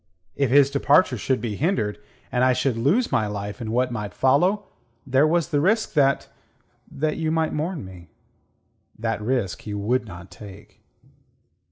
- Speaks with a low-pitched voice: Yes, low, 130 Hz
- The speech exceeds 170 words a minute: No, average, 165 wpm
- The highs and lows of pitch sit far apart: Yes, wide, 6.3 semitones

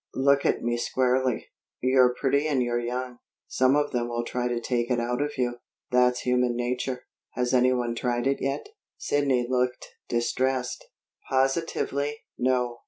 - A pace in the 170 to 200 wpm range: No, average, 155 wpm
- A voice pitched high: No, low, 125 Hz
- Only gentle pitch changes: Yes, narrow, 1.4 semitones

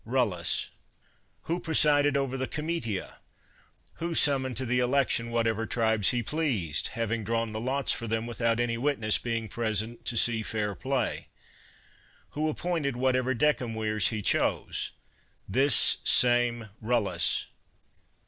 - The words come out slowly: Yes, slow, 130 wpm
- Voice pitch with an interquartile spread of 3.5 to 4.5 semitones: No, average, 3.1 semitones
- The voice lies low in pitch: Yes, low, 120 Hz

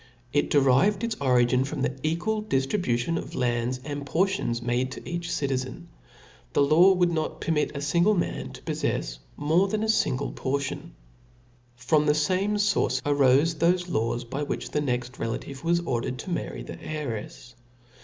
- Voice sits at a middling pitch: Yes, medium, 145 Hz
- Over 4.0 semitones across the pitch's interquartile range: Yes, average, 5.2 semitones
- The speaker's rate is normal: Yes, average, 165 wpm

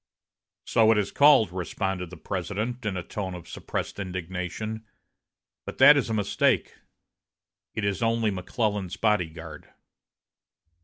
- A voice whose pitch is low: Yes, low, 100 Hz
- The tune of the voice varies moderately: Yes, average, 3.3 semitones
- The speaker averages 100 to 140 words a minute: Yes, slow, 135 wpm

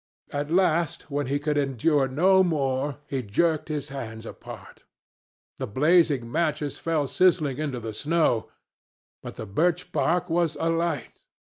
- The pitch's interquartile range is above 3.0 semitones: Yes, average, 3.7 semitones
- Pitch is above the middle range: No, medium, 150 Hz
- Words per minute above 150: No, average, 140 wpm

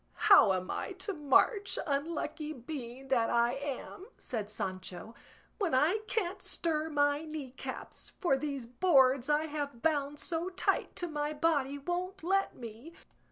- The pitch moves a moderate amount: Yes, average, 4.5 semitones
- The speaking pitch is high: Yes, very high, 295 Hz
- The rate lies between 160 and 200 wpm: No, average, 150 wpm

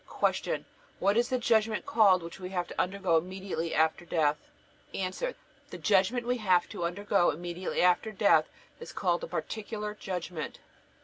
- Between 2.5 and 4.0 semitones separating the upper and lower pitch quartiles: Yes, average, 3.5 semitones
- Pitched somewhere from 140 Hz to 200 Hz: Yes, high, 190 Hz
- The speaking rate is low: No, average, 160 wpm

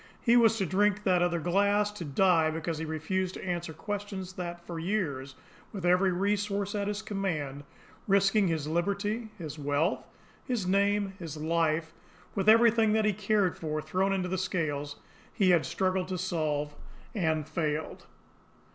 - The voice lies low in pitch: No, medium, 185 Hz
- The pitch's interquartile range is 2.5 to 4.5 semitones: Yes, average, 4.1 semitones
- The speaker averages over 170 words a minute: No, average, 160 wpm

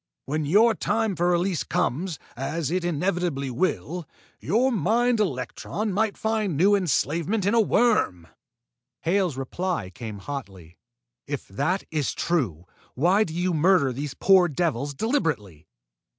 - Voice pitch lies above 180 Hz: No, medium, 170 Hz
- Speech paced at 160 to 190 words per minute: No, slow, 135 wpm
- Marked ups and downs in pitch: Yes, wide, 6.3 semitones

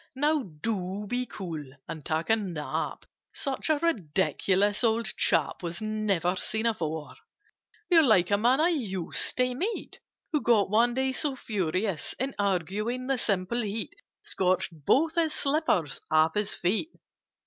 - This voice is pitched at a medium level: No, high, 215 Hz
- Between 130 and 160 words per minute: Yes, average, 150 wpm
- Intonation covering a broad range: Yes, wide, 5.9 semitones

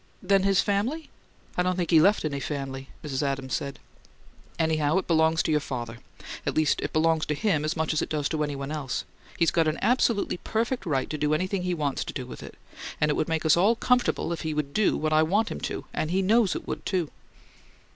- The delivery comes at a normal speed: No, fast, 235 wpm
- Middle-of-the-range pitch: Yes, medium, 160 Hz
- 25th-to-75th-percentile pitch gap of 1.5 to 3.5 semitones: No, average, 4.0 semitones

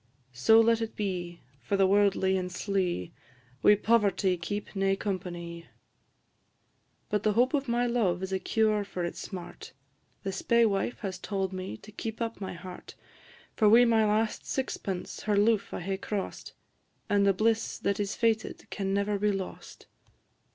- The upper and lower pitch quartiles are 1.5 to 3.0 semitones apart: Yes, average, 2.7 semitones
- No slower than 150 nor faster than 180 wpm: Yes, average, 165 wpm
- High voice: Yes, high, 200 Hz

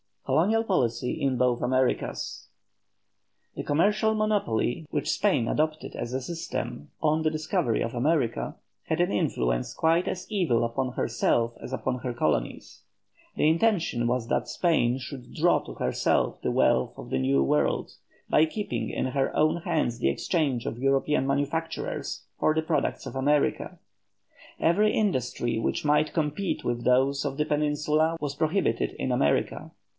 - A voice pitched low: No, medium, 145 Hz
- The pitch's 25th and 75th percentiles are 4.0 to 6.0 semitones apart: Yes, average, 5.0 semitones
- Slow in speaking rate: No, average, 150 wpm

